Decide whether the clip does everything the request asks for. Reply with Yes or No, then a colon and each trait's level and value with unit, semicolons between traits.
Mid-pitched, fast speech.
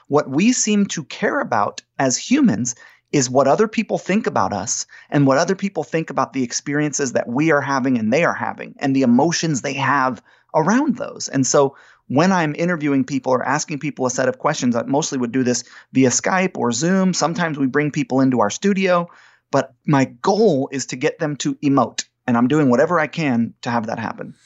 Yes: medium, 145 Hz; fast, 210 wpm